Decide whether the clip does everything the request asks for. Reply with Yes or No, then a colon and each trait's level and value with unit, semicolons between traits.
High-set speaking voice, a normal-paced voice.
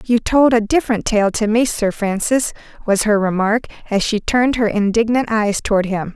Yes: high, 220 Hz; average, 195 wpm